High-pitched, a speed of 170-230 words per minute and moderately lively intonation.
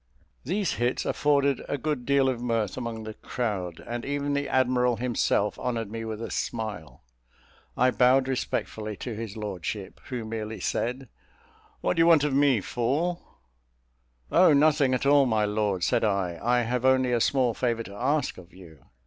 No: low, 120 Hz; average, 175 wpm; average, 3.9 semitones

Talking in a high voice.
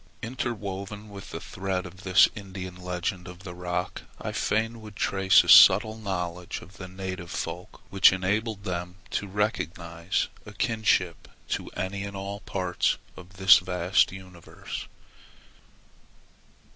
No: very low, 95 Hz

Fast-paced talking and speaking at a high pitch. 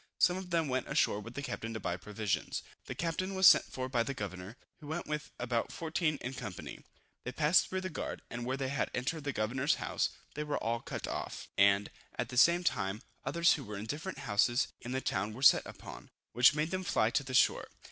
No: fast, 230 wpm; low, 130 Hz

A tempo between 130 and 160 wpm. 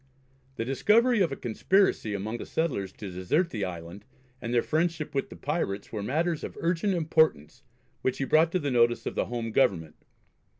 No: average, 185 wpm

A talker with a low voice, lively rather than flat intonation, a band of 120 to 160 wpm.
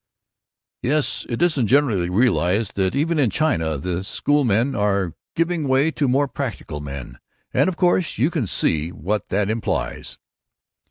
Yes: low, 115 Hz; wide, 7.8 semitones; average, 150 wpm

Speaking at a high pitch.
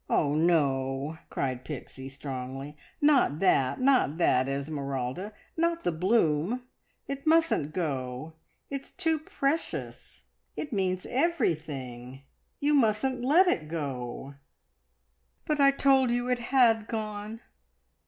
No: medium, 180 Hz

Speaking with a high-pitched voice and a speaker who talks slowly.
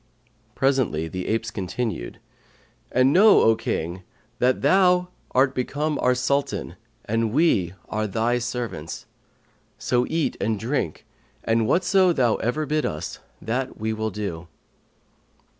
No: low, 120 Hz; slow, 125 wpm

